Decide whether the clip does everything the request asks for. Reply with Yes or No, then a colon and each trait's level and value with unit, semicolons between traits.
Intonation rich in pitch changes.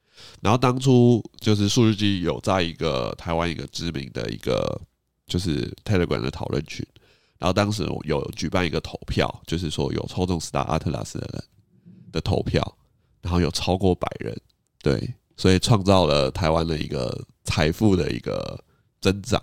No: average, 4.6 semitones